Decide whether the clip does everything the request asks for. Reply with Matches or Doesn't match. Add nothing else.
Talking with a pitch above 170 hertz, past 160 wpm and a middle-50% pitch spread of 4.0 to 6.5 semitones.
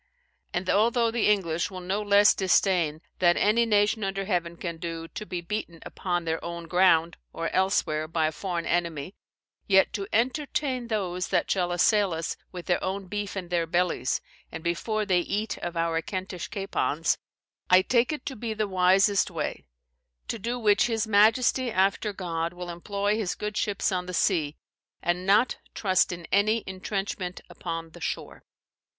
Doesn't match